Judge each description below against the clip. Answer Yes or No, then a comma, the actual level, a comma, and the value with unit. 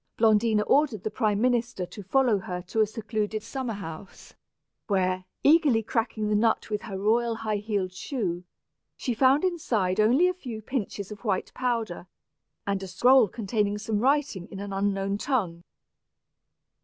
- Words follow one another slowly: No, average, 160 wpm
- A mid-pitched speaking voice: No, high, 215 Hz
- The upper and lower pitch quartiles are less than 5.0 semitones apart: Yes, average, 3.5 semitones